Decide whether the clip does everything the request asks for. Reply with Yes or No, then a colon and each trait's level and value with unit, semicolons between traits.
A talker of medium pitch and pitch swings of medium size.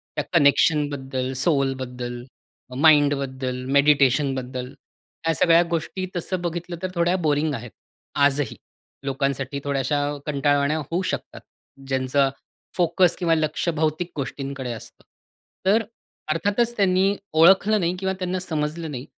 Yes: medium, 150 Hz; average, 4.2 semitones